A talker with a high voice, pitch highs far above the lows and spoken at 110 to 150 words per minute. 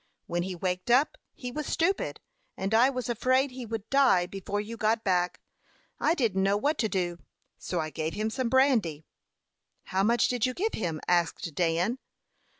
No: high, 215 Hz; wide, 5.9 semitones; average, 180 wpm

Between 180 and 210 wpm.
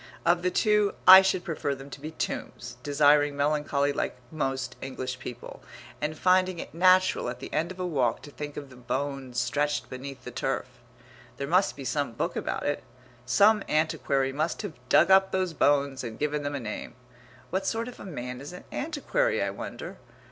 Yes: average, 190 wpm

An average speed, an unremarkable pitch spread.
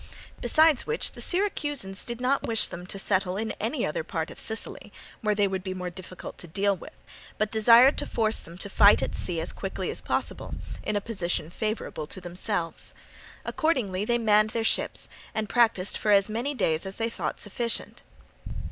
Yes: average, 190 wpm; average, 3.8 semitones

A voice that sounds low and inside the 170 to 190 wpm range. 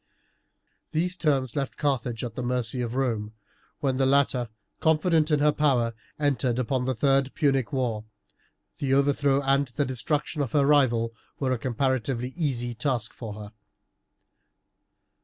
No: low, 130 Hz; average, 145 wpm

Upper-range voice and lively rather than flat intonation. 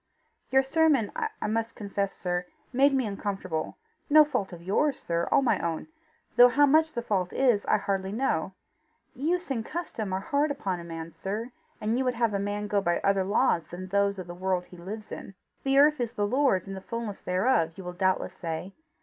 Yes: high, 205 Hz; wide, 5.9 semitones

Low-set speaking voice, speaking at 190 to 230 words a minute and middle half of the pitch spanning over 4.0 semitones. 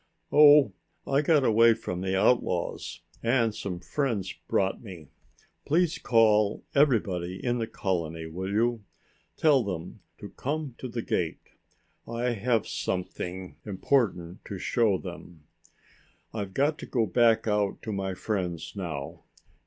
No: low, 105 Hz; slow, 135 wpm; average, 4.8 semitones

